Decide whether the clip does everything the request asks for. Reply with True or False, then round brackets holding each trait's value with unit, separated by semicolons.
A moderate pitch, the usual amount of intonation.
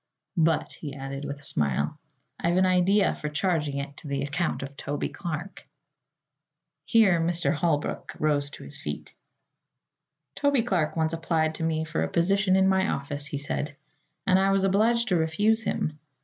True (165 Hz; 4.6 semitones)